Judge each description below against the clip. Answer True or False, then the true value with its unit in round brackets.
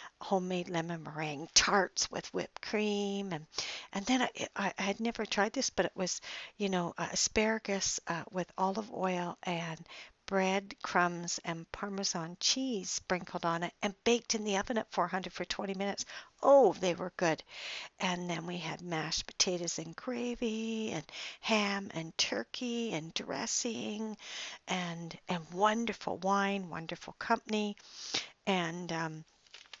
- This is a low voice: False (190 Hz)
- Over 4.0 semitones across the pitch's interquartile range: False (3.7 semitones)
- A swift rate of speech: False (145 wpm)